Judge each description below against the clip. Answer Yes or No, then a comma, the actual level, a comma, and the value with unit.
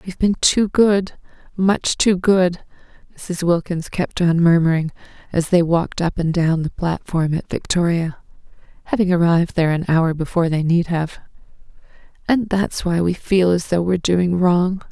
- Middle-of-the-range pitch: Yes, medium, 175 Hz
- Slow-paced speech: No, average, 160 wpm